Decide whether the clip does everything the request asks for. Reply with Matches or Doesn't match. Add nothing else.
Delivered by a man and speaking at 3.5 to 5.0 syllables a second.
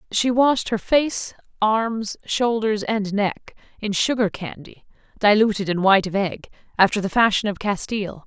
Doesn't match